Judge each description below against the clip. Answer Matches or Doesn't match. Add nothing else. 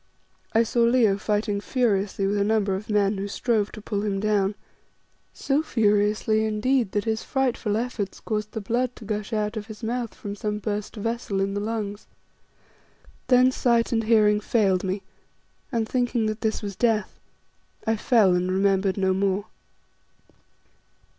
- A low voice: Doesn't match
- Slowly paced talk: Doesn't match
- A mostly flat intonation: Matches